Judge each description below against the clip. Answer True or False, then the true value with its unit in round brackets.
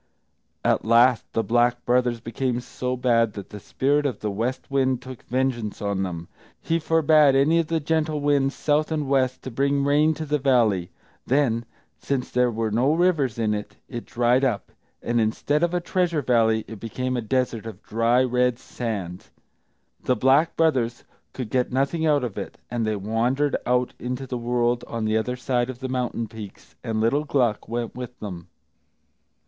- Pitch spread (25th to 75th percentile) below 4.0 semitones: True (3.3 semitones)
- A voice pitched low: True (125 Hz)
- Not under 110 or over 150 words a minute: False (185 wpm)